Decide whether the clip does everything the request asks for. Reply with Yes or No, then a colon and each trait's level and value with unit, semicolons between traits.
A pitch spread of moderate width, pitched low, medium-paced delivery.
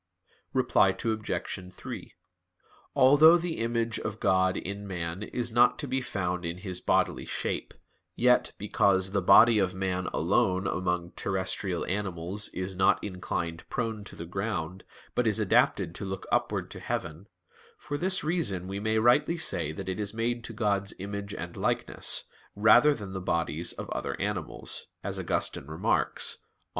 Yes: average, 3.8 semitones; low, 100 Hz; average, 160 wpm